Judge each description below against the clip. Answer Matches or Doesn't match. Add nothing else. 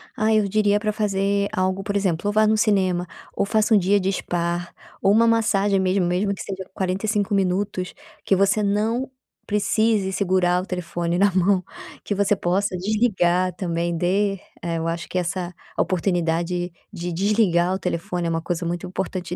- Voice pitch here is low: Doesn't match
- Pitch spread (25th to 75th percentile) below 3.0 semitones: Matches